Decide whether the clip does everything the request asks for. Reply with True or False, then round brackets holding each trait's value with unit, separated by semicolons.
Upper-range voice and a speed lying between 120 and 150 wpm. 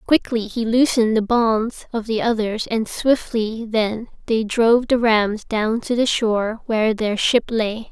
False (225 Hz; 175 wpm)